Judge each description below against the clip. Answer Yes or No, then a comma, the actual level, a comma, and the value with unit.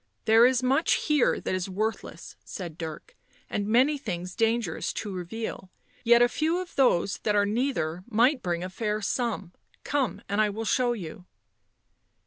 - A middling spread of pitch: Yes, average, 4.9 semitones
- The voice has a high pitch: Yes, high, 220 Hz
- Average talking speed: Yes, average, 180 wpm